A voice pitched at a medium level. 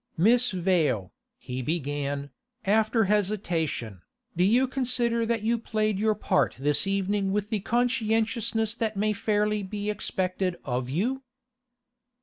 No: high, 205 Hz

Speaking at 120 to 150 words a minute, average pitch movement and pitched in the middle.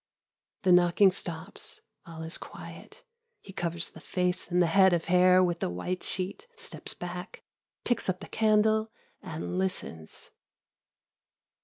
No: average, 140 wpm; narrow, 2.0 semitones; medium, 180 Hz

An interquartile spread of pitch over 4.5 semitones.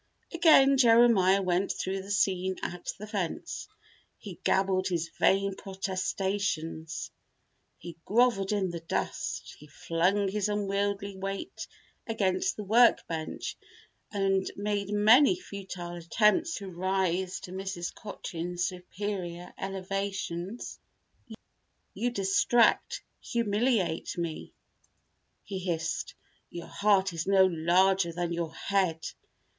No: narrow, 2.5 semitones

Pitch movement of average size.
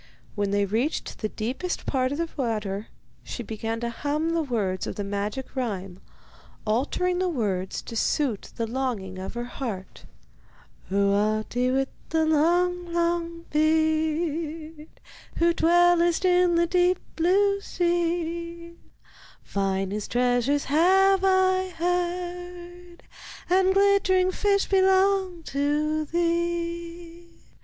No: wide, 6.6 semitones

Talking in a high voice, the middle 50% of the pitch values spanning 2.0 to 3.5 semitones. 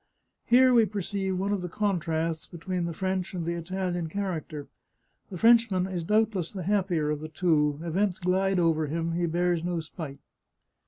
No: medium, 180 Hz; average, 2.8 semitones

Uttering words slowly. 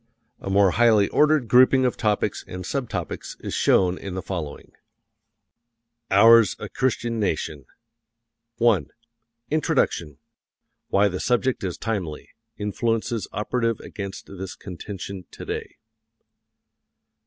Yes: slow, 110 wpm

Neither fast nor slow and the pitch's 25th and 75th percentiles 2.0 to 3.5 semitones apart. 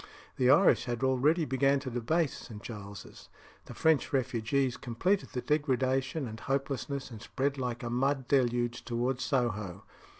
Yes: average, 145 wpm; narrow, 2.6 semitones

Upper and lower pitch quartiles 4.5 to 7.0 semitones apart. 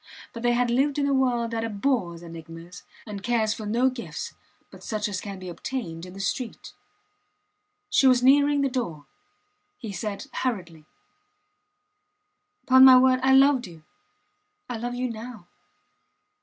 Yes: average, 4.8 semitones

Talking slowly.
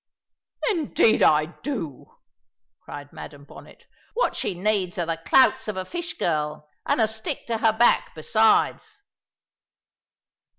Yes: slow, 130 wpm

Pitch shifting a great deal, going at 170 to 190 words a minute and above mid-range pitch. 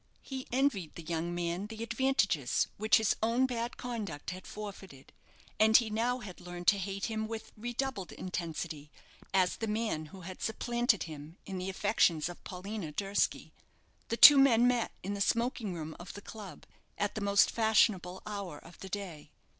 No: average, 4.3 semitones; average, 175 wpm; high, 200 Hz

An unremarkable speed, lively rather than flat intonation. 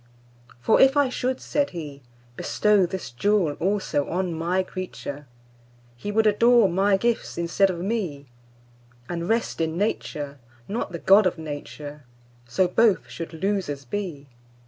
No: slow, 125 wpm; wide, 7.6 semitones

